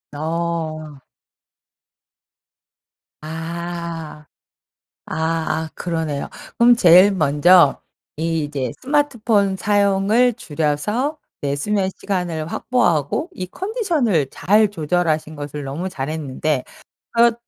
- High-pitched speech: No, medium, 170 Hz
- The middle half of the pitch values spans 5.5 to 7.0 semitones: No, average, 5.1 semitones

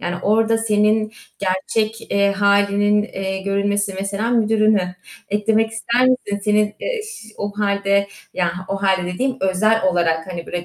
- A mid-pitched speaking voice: No, high, 205 Hz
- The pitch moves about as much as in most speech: No, narrow, 2.1 semitones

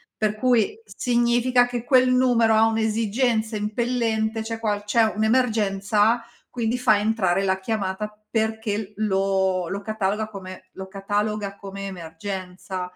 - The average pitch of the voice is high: Yes, high, 215 Hz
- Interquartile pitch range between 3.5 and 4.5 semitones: No, average, 2.7 semitones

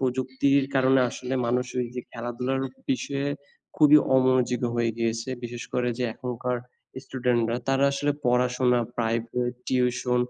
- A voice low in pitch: Yes, low, 125 Hz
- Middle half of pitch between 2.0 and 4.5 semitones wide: No, narrow, 1.4 semitones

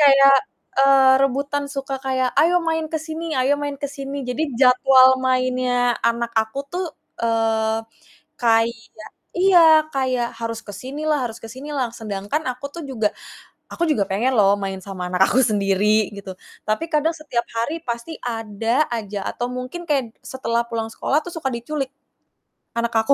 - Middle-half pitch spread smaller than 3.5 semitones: No, average, 3.8 semitones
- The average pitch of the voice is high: Yes, very high, 255 Hz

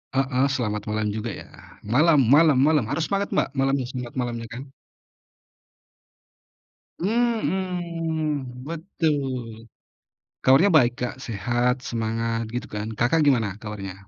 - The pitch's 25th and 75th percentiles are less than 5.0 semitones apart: No, wide, 5.5 semitones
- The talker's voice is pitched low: Yes, low, 130 Hz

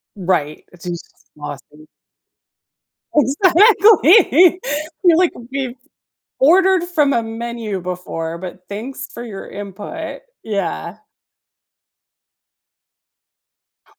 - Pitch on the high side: Yes, high, 235 Hz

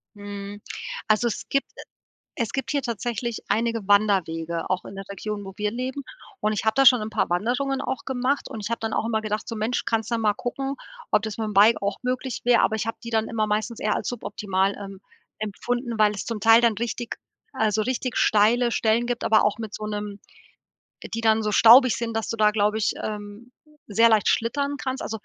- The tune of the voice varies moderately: No, narrow, 2.3 semitones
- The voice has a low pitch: No, high, 220 Hz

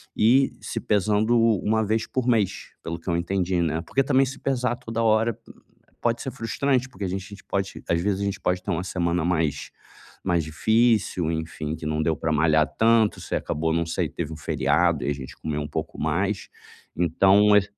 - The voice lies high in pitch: No, very low, 95 Hz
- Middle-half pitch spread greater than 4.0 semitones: Yes, wide, 5.5 semitones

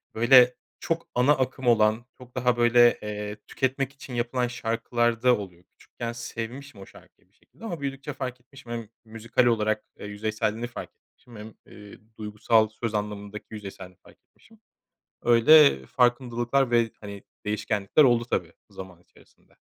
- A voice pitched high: No, low, 120 Hz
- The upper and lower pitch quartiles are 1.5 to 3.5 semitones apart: Yes, average, 2.8 semitones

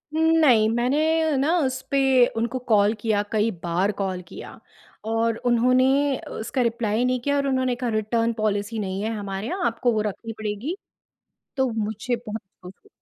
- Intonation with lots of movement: No, average, 3.2 semitones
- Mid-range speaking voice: No, high, 230 Hz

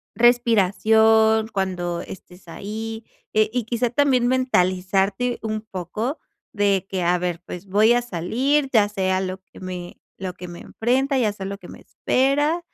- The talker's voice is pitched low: No, high, 215 Hz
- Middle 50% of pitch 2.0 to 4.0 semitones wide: No, average, 4.5 semitones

